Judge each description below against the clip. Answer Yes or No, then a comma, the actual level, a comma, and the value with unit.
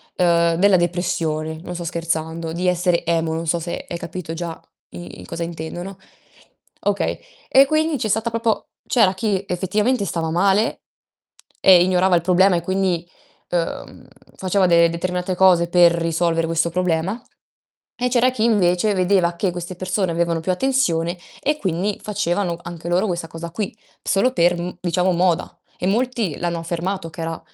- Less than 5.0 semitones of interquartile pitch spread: Yes, narrow, 2.4 semitones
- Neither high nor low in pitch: Yes, medium, 175 Hz